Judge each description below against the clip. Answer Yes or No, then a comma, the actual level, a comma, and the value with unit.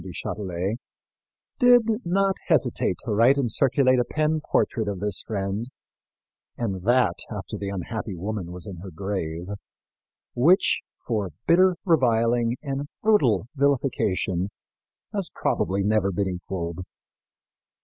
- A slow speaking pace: Yes, slow, 125 wpm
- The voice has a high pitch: No, low, 110 Hz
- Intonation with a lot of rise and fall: Yes, wide, 6.2 semitones